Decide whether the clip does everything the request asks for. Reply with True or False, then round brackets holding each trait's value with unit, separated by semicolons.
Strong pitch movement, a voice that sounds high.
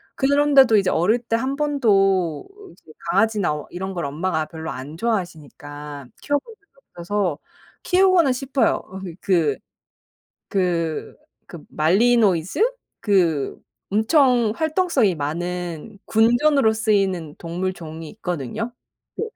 True (6.7 semitones; 195 Hz)